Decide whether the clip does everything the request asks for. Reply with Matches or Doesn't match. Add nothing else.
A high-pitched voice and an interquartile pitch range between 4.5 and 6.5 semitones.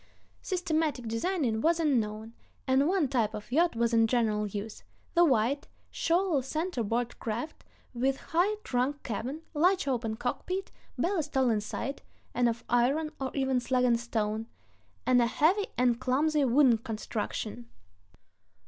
Matches